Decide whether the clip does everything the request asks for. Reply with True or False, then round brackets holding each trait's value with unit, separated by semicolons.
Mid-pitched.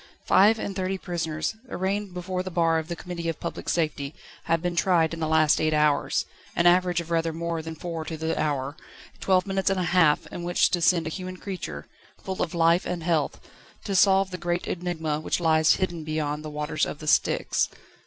True (170 Hz)